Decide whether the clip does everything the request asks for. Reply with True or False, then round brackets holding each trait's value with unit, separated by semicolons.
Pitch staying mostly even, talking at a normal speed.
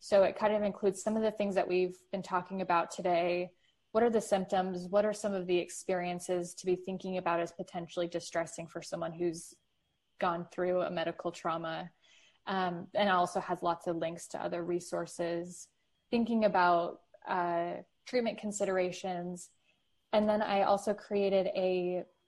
True (2.3 semitones; 165 wpm)